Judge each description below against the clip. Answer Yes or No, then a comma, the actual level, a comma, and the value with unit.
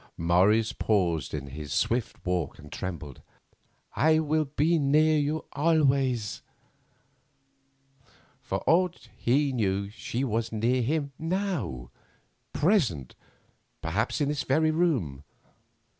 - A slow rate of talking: Yes, slow, 105 wpm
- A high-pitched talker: No, low, 130 Hz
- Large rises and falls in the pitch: Yes, wide, 8.7 semitones